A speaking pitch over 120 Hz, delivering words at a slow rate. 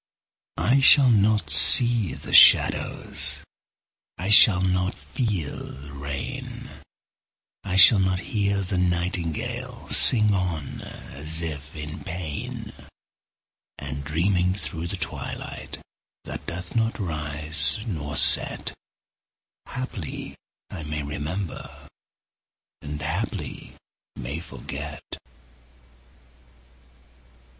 No: very low, 90 Hz; slow, 95 wpm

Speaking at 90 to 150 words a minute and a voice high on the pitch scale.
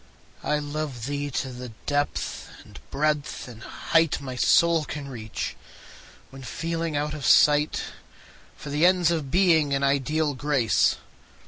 No: average, 140 wpm; medium, 145 Hz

